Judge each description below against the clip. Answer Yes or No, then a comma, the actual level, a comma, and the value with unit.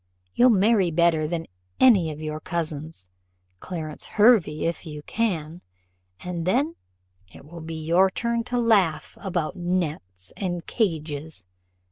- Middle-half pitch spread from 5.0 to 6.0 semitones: No, average, 3.9 semitones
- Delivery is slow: Yes, slow, 130 wpm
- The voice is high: No, medium, 170 Hz